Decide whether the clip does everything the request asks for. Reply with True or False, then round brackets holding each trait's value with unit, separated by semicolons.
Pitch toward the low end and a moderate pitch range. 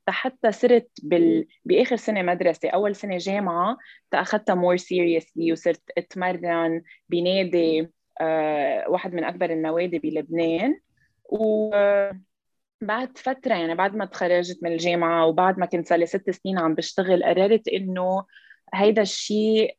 False (180 Hz; 3.9 semitones)